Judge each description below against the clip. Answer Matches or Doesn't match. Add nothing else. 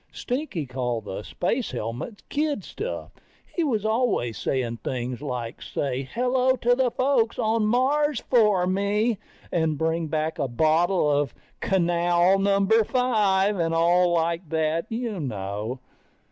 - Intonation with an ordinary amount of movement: Doesn't match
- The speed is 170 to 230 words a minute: Doesn't match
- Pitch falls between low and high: Matches